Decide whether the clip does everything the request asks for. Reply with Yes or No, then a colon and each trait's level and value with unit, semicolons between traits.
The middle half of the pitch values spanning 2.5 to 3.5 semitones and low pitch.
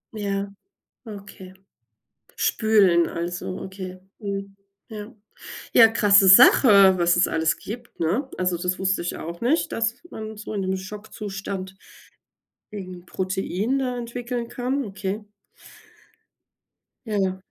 No: average, 2.9 semitones; high, 200 Hz